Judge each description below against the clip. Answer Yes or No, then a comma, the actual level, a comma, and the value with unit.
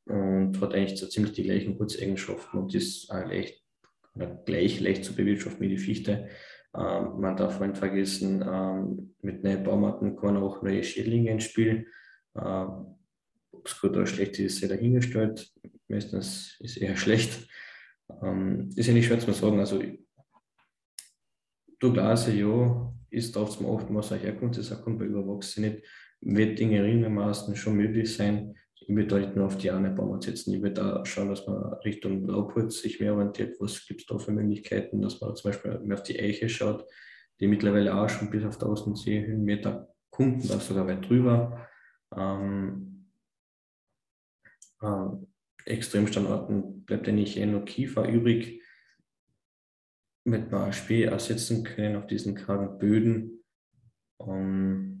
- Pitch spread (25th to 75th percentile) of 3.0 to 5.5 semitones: No, narrow, 2.4 semitones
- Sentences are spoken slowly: No, average, 155 wpm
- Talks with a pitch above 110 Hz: No, low, 105 Hz